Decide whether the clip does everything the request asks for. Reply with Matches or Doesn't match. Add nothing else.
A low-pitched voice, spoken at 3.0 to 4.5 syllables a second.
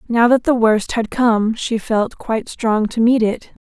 Doesn't match